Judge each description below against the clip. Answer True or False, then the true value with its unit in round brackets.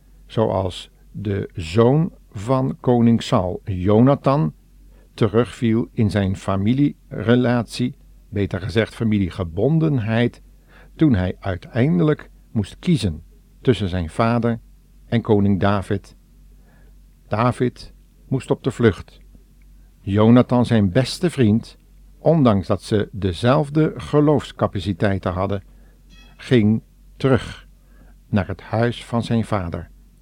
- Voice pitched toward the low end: True (110 Hz)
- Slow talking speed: True (95 wpm)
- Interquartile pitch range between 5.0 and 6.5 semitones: False (4.6 semitones)